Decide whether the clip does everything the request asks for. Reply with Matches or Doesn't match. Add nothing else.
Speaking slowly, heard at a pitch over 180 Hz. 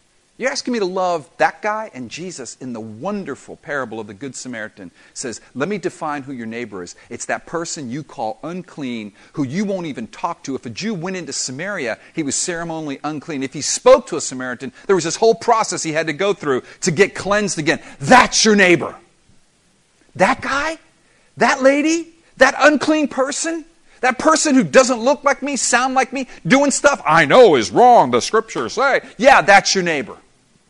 Doesn't match